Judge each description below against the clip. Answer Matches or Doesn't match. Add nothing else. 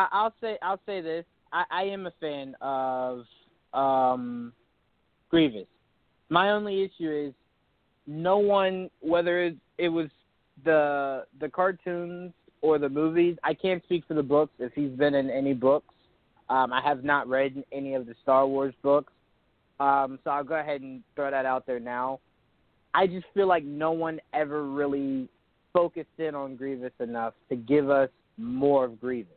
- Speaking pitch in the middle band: Matches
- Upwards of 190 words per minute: Doesn't match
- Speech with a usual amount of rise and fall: Matches